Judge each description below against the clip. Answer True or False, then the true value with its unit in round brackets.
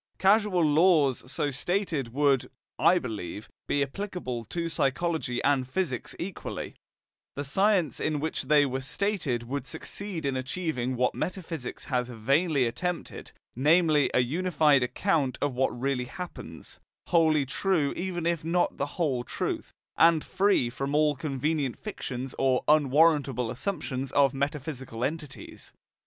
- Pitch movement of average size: True (4.6 semitones)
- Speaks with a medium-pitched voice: True (145 Hz)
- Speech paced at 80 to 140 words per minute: True (135 wpm)